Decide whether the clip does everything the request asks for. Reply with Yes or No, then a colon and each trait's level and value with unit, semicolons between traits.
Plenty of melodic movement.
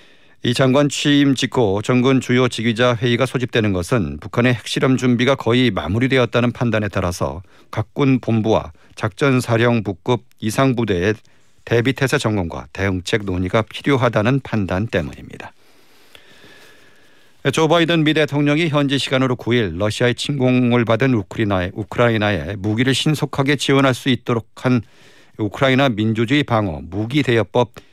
No: average, 3.8 semitones